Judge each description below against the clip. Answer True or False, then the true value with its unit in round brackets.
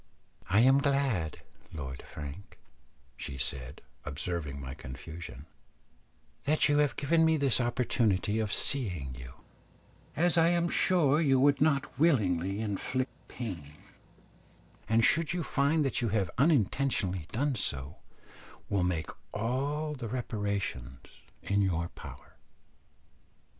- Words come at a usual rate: False (120 wpm)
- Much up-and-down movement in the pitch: True (8.7 semitones)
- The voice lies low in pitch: True (110 Hz)